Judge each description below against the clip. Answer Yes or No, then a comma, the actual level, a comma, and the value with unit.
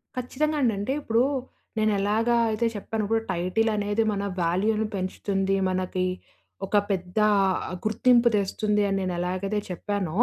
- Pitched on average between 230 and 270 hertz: No, high, 205 Hz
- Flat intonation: No, average, 3.0 semitones